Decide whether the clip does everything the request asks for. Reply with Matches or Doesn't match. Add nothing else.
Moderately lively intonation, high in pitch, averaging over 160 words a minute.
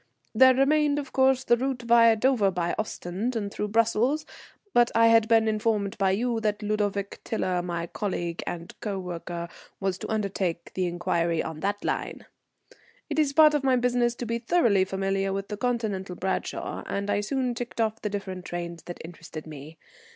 Matches